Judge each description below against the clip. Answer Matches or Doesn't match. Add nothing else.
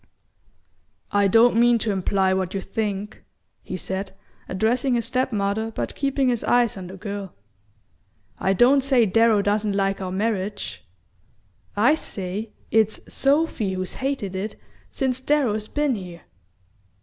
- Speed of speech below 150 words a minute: Matches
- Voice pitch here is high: Matches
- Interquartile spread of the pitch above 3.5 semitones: Matches